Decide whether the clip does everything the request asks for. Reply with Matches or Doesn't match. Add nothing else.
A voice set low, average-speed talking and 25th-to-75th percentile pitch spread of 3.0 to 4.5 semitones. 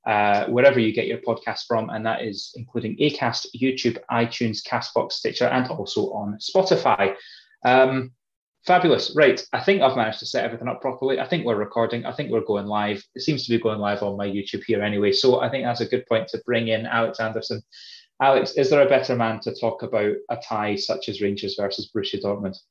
Doesn't match